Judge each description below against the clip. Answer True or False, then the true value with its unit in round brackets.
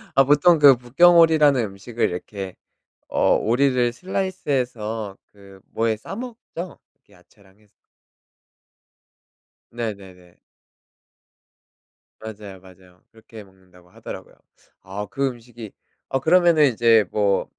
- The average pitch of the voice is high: False (115 Hz)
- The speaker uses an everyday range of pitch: False (6.1 semitones)